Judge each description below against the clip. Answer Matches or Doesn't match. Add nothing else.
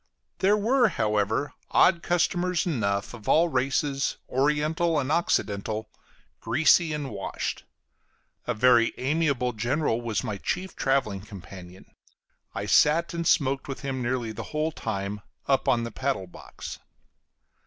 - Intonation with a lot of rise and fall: Matches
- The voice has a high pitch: Doesn't match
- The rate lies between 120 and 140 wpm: Matches